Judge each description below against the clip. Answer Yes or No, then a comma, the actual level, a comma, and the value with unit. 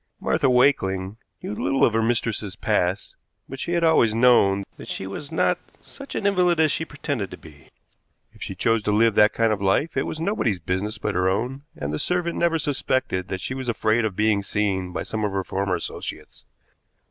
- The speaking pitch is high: No, low, 110 Hz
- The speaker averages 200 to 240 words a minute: Yes, fast, 205 wpm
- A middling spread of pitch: No, wide, 6.1 semitones